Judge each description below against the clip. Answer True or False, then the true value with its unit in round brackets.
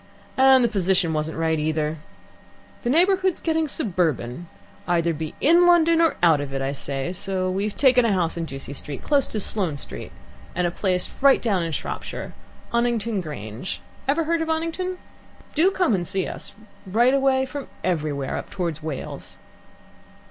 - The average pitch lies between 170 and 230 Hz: True (190 Hz)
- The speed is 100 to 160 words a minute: False (170 wpm)